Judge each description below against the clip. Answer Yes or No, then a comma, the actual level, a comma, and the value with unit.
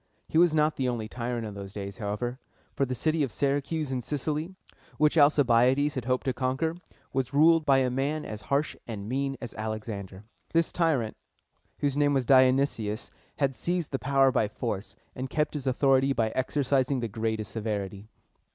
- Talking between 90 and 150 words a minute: No, average, 185 wpm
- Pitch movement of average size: Yes, average, 4.1 semitones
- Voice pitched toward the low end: Yes, low, 130 Hz